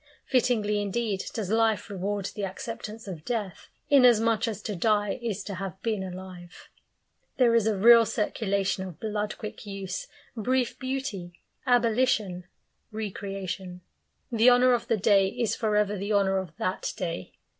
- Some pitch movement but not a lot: Yes, average, 3.1 semitones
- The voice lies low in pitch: No, high, 210 Hz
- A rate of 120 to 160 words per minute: Yes, average, 150 wpm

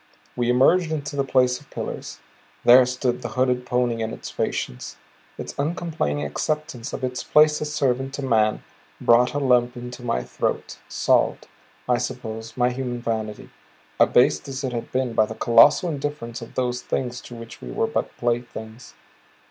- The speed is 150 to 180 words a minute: Yes, average, 170 wpm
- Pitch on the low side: Yes, low, 125 Hz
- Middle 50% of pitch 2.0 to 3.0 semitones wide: Yes, narrow, 2.5 semitones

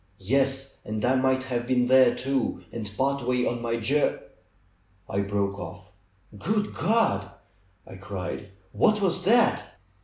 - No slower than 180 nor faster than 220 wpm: No, average, 150 wpm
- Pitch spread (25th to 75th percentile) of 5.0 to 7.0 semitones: Yes, average, 5.3 semitones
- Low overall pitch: Yes, low, 125 Hz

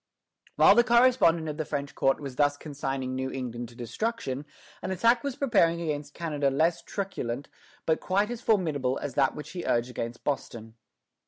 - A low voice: No, medium, 145 Hz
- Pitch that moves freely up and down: Yes, wide, 6.0 semitones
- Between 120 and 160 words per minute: No, average, 175 wpm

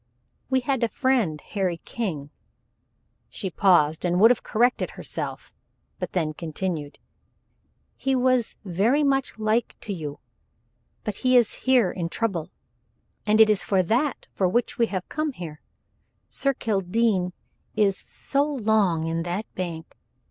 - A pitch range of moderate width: No, wide, 5.7 semitones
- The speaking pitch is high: Yes, high, 205 Hz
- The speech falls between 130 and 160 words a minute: Yes, average, 140 wpm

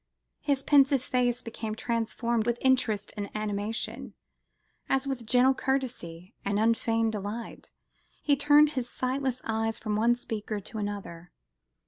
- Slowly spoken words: Yes, slow, 130 wpm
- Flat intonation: No, average, 3.5 semitones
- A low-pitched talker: No, high, 230 Hz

